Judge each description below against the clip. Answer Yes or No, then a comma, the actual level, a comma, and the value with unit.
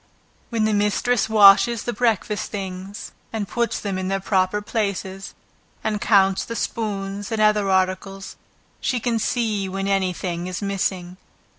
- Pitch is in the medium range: No, high, 200 Hz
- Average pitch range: No, narrow, 2.2 semitones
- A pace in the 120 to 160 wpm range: Yes, average, 150 wpm